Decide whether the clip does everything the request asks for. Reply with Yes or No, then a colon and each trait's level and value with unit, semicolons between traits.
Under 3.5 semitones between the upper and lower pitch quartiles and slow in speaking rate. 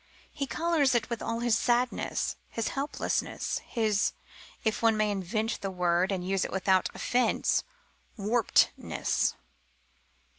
No: average, 3.8 semitones; slow, 125 wpm